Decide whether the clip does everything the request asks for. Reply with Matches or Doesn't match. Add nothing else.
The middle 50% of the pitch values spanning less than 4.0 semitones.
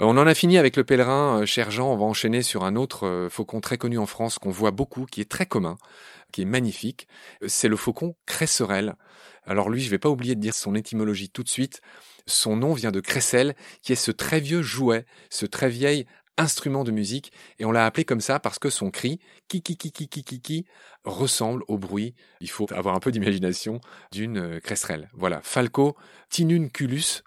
Doesn't match